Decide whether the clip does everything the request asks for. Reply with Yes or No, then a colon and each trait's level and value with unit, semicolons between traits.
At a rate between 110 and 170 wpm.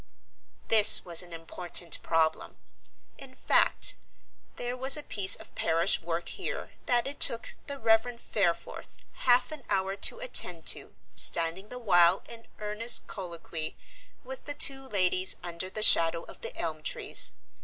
Yes: average, 150 wpm